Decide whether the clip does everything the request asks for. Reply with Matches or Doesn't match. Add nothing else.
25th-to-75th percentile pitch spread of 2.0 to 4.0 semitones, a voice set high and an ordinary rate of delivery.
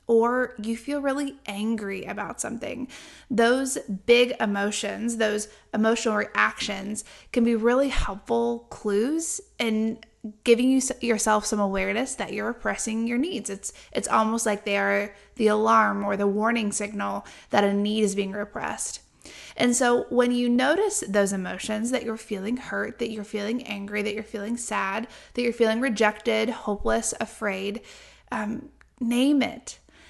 Matches